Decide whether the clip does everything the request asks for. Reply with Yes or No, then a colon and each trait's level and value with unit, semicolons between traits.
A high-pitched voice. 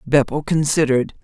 No: medium, 145 Hz